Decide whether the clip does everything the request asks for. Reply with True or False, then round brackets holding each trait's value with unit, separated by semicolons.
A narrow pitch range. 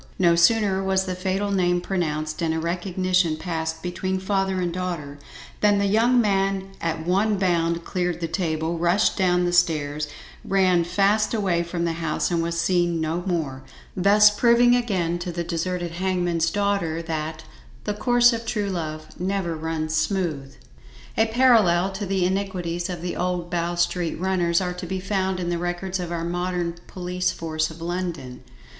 True (2.3 semitones)